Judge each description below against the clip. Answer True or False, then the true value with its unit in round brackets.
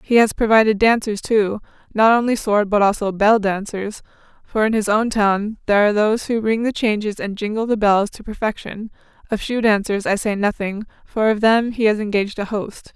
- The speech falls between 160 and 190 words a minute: False (205 wpm)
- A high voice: True (215 Hz)